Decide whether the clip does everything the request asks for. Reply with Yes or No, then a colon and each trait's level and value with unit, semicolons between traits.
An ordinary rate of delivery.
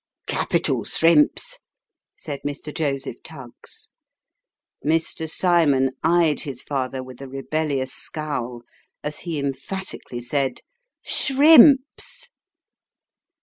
No: slow, 105 wpm